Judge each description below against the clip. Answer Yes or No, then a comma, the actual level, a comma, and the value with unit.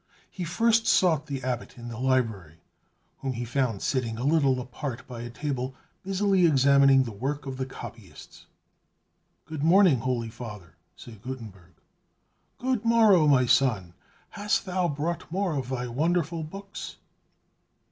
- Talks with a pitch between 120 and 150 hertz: Yes, low, 135 Hz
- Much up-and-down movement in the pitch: Yes, wide, 5.8 semitones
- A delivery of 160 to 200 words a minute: No, average, 145 wpm